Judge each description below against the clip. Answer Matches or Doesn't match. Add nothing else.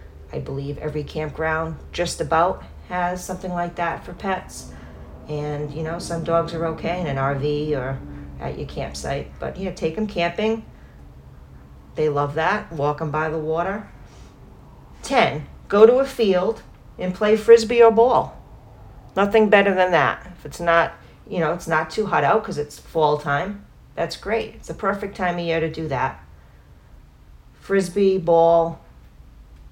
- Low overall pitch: Doesn't match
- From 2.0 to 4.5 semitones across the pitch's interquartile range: Doesn't match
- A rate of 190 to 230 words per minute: Doesn't match